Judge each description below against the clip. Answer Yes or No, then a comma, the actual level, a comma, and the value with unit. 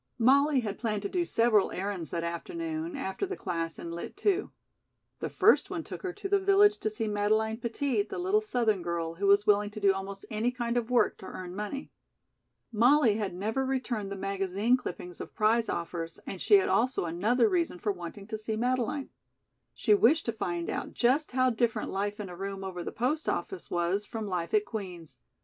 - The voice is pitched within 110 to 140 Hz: No, high, 215 Hz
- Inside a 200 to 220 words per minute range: Yes, fast, 205 wpm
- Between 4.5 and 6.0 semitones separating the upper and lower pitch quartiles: Yes, average, 4.9 semitones